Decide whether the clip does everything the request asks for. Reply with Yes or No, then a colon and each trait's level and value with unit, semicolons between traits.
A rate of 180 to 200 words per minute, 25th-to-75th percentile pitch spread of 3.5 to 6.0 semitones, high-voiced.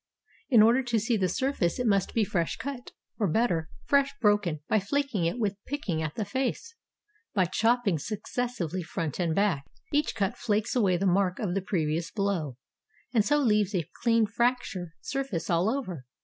Yes: average, 185 wpm; wide, 5.5 semitones; high, 205 Hz